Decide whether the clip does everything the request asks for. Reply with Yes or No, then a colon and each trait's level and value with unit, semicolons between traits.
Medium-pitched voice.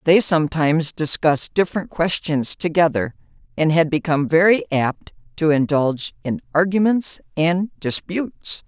Yes: medium, 165 Hz